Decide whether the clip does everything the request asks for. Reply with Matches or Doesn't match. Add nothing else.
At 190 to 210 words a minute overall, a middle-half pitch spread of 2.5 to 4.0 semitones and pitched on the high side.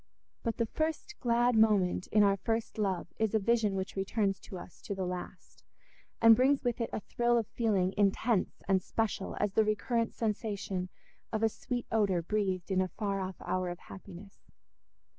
Doesn't match